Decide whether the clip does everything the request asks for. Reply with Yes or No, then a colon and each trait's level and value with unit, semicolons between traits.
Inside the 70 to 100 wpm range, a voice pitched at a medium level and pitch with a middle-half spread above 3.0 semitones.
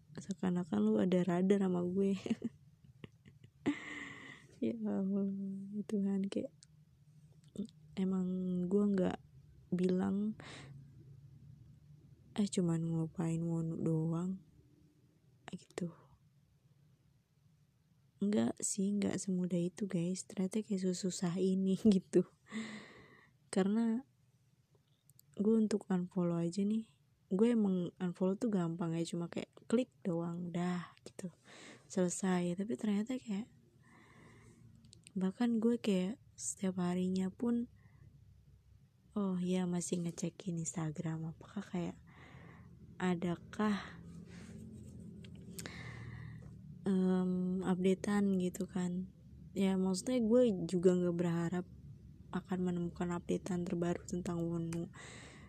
Yes: average, 90 wpm; medium, 180 Hz; average, 4.2 semitones